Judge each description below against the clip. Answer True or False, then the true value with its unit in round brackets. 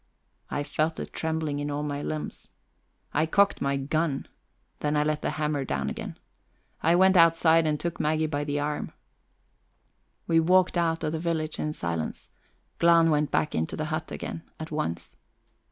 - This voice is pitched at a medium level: True (155 Hz)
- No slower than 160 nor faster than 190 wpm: True (170 wpm)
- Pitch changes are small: True (1.9 semitones)